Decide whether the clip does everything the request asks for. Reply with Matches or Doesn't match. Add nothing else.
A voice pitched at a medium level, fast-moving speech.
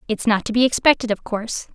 Doesn't match